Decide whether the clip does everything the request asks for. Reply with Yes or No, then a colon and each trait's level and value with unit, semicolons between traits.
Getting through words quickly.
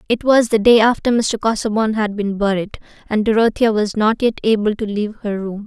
Yes: fast, 210 wpm